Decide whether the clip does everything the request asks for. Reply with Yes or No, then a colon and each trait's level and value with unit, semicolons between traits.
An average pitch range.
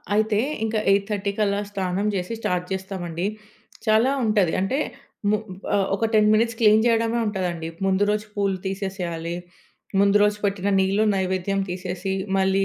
No: narrow, 2.0 semitones